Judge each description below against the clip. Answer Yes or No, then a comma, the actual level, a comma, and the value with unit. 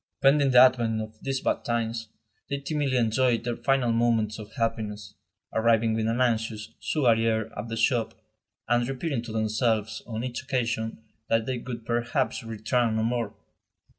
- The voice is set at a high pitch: No, low, 115 Hz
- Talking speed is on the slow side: No, average, 165 wpm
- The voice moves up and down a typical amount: No, narrow, 2.0 semitones